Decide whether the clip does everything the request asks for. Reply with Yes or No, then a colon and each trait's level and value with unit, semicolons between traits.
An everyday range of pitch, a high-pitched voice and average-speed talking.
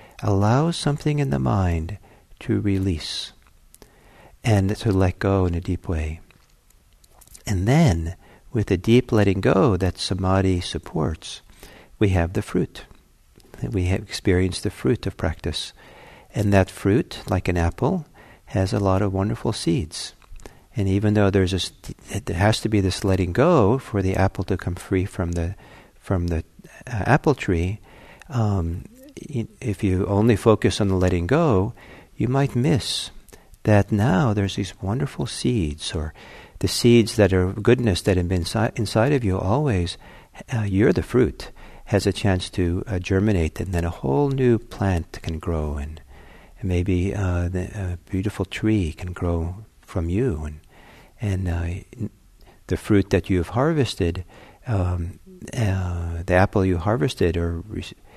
No: average, 3.3 semitones; very low, 95 Hz; average, 155 wpm